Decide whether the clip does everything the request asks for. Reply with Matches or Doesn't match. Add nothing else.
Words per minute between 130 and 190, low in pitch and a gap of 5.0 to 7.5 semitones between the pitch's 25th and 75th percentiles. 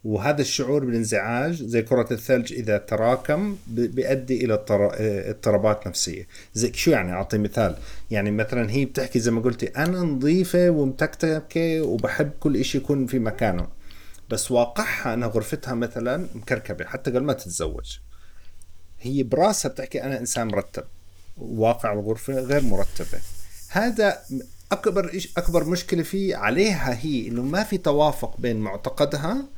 Matches